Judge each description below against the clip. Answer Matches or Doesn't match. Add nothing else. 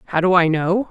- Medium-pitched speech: Matches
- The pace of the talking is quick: Matches